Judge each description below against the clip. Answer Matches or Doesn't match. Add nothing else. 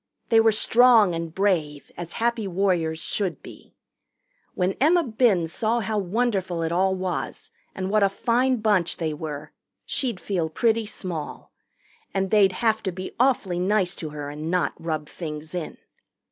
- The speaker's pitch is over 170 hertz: Matches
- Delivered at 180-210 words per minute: Doesn't match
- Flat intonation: Doesn't match